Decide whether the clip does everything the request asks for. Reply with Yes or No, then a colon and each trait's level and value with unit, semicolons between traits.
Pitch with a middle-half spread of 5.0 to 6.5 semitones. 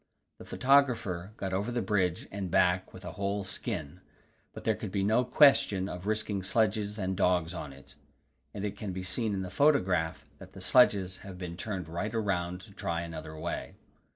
No: average, 2.8 semitones